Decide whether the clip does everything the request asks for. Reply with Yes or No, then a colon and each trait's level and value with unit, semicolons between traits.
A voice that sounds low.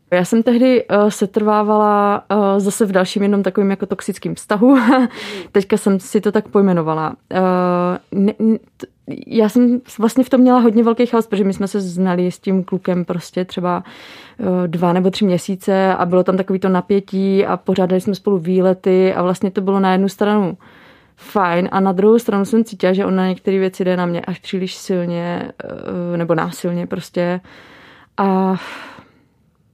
No: high, 195 Hz